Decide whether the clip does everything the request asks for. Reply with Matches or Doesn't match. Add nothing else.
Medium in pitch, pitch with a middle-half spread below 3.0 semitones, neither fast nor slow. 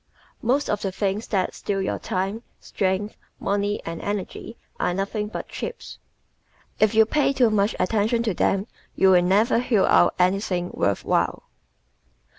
Doesn't match